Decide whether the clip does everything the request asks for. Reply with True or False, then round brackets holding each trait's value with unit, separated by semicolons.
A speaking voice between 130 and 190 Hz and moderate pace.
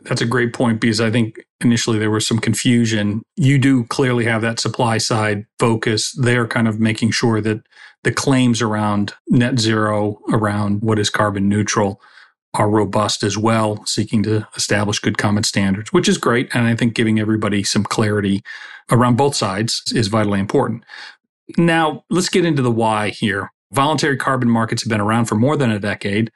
False (115 Hz; 180 wpm)